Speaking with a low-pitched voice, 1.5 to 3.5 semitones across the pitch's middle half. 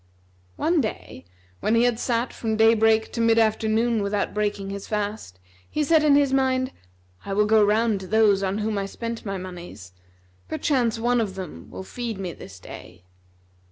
No: high, 220 Hz; average, 3.0 semitones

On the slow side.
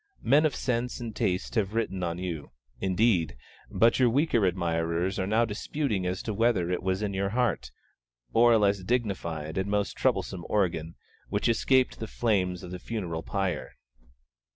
No: average, 165 wpm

